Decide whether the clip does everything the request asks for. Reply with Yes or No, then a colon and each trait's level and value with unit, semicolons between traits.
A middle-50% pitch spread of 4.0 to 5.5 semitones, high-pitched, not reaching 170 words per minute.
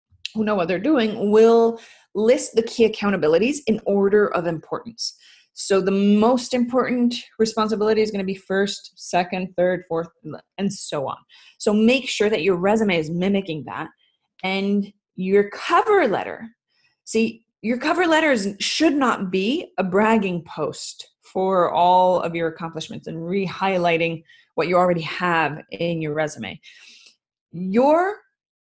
Yes: average, 4.3 semitones; high, 200 Hz; average, 140 wpm